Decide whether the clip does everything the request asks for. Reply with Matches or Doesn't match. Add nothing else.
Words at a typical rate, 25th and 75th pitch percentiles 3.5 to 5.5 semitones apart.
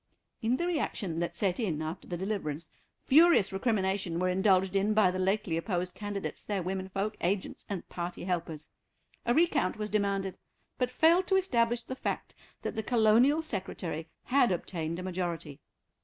Matches